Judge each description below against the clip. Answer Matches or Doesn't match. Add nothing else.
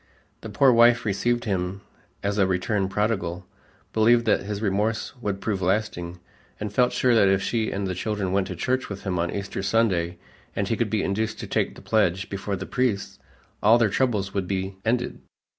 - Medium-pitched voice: Doesn't match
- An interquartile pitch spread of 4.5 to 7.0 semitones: Doesn't match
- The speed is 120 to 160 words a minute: Doesn't match